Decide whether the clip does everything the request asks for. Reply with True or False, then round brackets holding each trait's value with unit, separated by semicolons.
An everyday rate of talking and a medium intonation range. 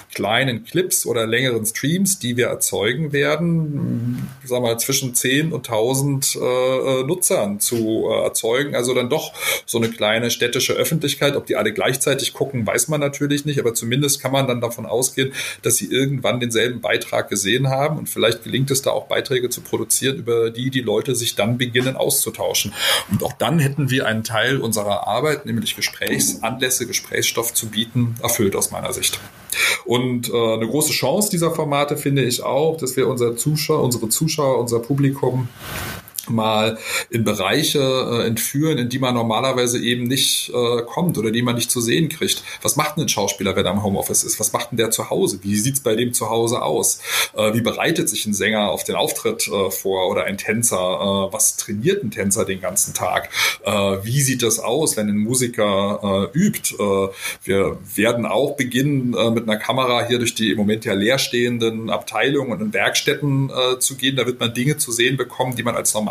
False (195 wpm; 3.3 semitones)